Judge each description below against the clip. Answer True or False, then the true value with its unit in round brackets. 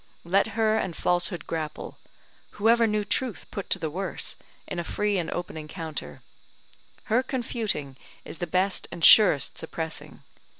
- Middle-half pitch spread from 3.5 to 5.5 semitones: True (4.7 semitones)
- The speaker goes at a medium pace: True (155 wpm)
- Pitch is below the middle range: False (180 Hz)